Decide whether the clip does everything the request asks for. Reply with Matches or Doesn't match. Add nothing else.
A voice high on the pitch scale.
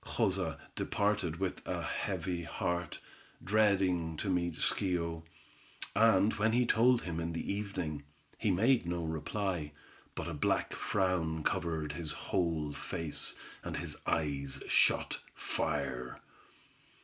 Doesn't match